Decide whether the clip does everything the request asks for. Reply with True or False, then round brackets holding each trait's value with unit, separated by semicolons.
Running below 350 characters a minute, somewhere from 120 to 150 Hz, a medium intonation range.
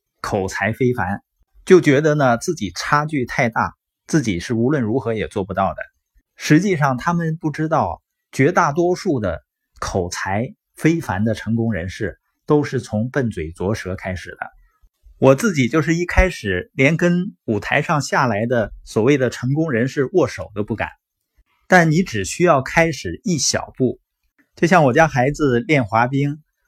False (235 characters per minute; 135 Hz; 6.2 semitones)